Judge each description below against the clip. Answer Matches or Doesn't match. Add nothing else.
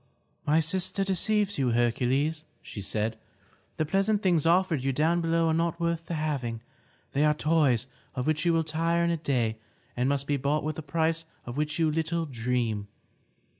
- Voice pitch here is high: Doesn't match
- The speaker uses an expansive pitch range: Doesn't match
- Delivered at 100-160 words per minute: Doesn't match